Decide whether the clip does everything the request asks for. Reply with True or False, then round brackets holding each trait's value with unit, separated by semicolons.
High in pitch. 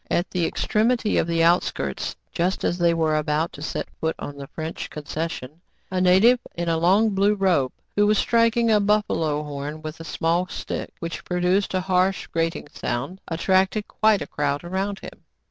False (175 Hz)